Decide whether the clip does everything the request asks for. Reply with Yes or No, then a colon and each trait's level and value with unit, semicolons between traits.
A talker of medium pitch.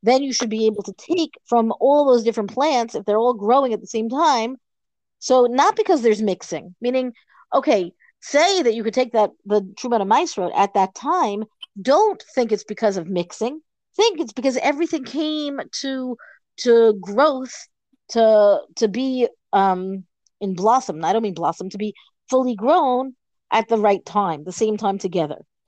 No: high, 230 Hz